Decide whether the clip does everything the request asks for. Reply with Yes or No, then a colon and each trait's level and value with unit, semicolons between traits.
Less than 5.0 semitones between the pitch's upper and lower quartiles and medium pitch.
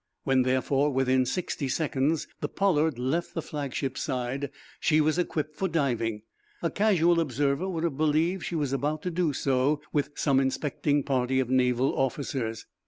Yes: average, 3.4 semitones; medium, 145 Hz